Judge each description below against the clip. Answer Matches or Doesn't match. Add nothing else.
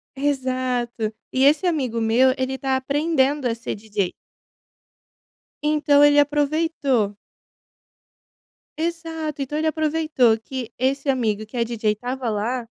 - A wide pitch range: Doesn't match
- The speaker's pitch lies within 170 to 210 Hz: Doesn't match